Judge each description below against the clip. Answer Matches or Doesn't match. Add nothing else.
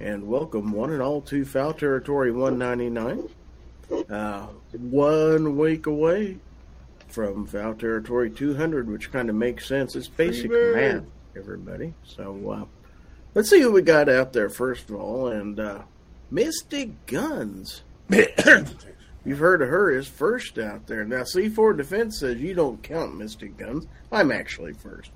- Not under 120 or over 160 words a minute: Matches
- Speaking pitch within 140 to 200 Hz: Doesn't match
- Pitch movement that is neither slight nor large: Doesn't match